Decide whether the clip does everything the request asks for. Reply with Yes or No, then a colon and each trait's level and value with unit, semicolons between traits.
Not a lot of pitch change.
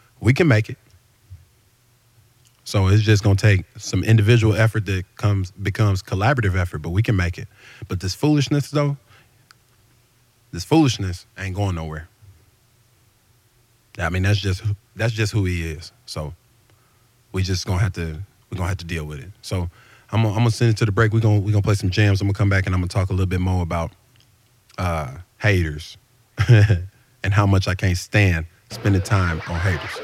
No: average, 3.7 semitones